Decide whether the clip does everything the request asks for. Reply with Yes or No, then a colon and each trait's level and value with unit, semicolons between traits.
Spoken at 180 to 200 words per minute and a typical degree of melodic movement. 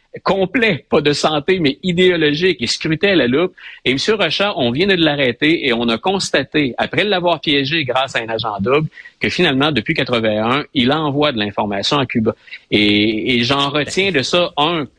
No: average, 185 wpm; wide, 5.9 semitones